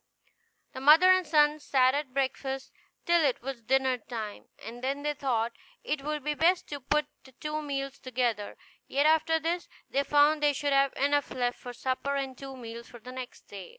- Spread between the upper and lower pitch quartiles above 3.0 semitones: No, average, 2.7 semitones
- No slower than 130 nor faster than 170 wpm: No, average, 195 wpm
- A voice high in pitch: Yes, very high, 275 Hz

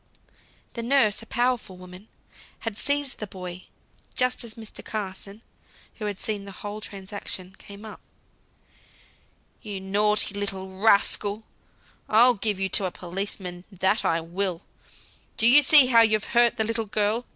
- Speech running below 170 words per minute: Yes, average, 150 wpm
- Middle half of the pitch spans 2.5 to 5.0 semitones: Yes, average, 2.8 semitones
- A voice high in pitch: Yes, high, 210 Hz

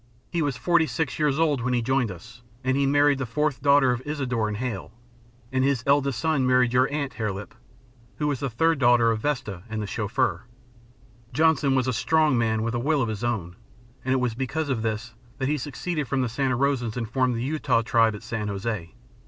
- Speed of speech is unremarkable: No, fast, 220 wpm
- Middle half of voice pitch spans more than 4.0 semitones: No, average, 3.7 semitones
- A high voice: No, low, 125 Hz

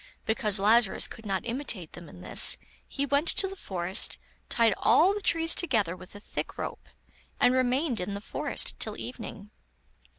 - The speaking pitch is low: No, high, 225 Hz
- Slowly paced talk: No, average, 170 wpm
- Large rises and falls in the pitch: Yes, wide, 6.2 semitones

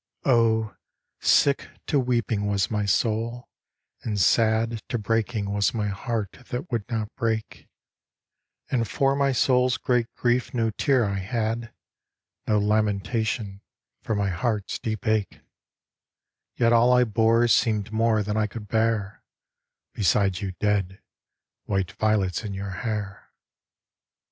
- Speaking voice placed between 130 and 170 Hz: No, low, 110 Hz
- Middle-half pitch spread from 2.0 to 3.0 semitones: Yes, narrow, 2.4 semitones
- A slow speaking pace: Yes, slow, 130 wpm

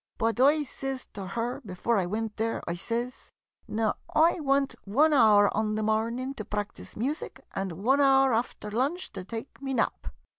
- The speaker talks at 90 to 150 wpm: No, average, 190 wpm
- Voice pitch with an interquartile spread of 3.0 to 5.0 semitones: Yes, average, 4.2 semitones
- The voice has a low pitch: No, high, 230 Hz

